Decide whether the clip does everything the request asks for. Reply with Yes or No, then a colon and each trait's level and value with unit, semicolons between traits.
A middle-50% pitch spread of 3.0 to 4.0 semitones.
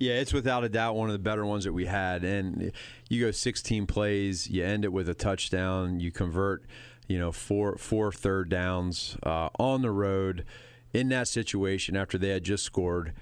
Yes: average, 3.3 semitones